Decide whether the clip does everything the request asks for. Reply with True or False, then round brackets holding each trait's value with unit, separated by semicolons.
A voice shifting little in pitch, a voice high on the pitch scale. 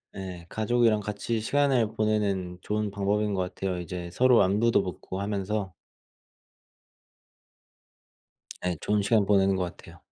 False (2.3 semitones; 100 Hz)